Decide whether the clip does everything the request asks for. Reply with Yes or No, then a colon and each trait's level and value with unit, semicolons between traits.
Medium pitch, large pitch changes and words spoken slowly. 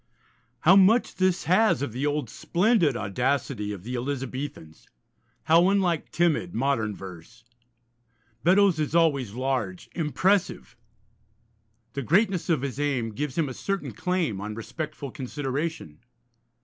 Yes: medium, 145 Hz; wide, 6.4 semitones; slow, 125 wpm